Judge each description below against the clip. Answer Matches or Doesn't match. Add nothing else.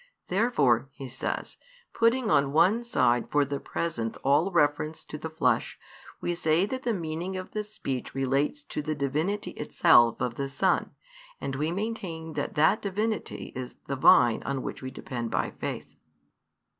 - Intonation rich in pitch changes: Matches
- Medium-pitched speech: Matches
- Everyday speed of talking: Matches